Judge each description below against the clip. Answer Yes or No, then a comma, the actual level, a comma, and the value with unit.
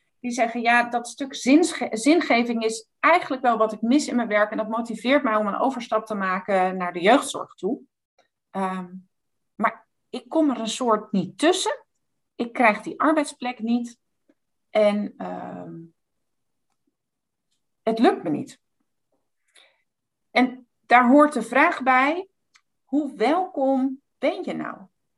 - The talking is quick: No, average, 140 wpm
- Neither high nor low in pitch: No, high, 240 Hz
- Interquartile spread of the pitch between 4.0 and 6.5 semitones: Yes, average, 4.4 semitones